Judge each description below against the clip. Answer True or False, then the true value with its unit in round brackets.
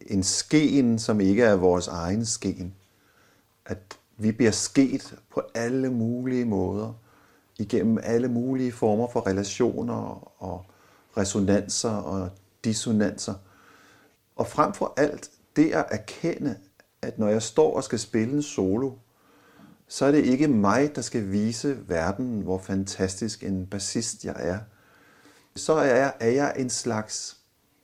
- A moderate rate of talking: False (140 wpm)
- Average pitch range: True (3.8 semitones)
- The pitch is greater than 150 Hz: False (110 Hz)